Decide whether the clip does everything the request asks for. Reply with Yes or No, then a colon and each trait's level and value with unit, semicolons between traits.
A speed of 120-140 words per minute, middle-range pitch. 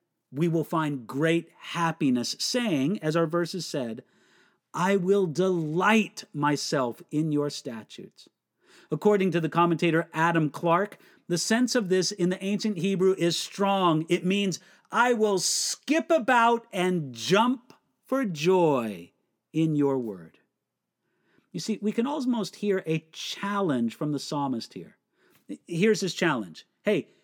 Yes: slow, 135 wpm; medium, 175 Hz